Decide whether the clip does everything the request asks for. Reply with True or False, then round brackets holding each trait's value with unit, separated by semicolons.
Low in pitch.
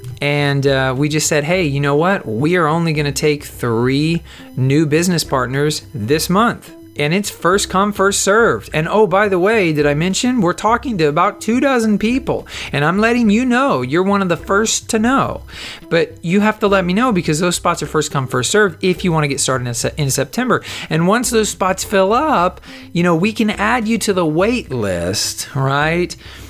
False (170 Hz)